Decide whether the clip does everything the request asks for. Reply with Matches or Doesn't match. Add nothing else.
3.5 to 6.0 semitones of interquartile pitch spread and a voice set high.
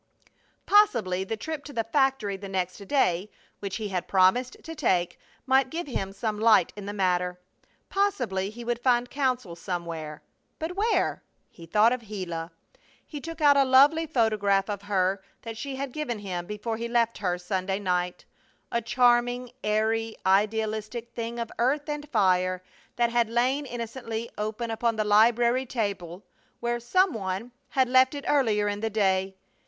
Matches